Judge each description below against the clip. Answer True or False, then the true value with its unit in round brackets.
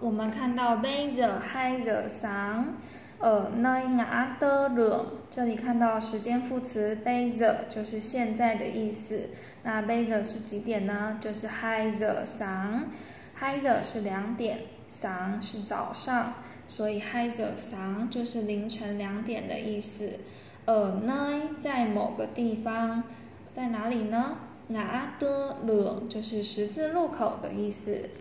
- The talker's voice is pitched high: True (225 Hz)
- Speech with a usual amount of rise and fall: False (2.3 semitones)